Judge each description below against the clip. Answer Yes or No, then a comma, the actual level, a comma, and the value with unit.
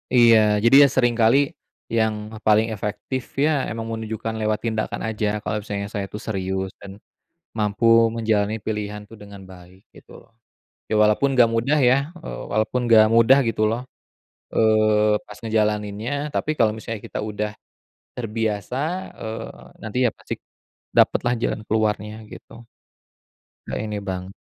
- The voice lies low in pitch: Yes, low, 110 Hz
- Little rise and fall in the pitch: Yes, narrow, 1.4 semitones